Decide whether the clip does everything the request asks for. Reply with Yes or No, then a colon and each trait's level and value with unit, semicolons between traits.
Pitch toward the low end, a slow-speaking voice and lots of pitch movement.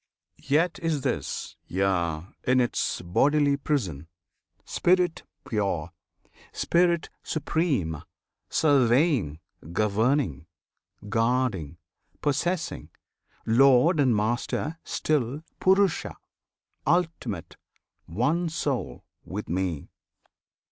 Yes: low, 130 Hz; slow, 80 wpm; wide, 8.3 semitones